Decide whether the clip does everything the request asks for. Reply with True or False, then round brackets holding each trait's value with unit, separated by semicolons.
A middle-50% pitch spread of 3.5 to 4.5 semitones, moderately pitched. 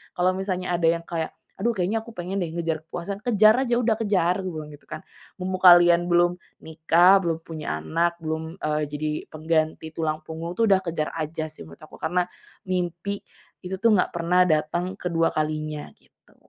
False (2.8 semitones; 170 Hz)